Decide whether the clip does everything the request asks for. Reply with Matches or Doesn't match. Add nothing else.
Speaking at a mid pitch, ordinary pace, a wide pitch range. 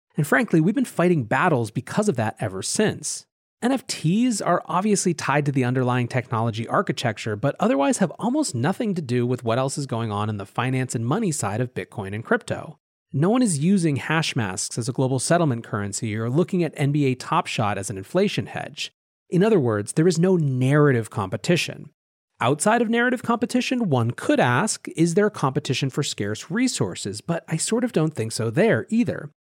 Matches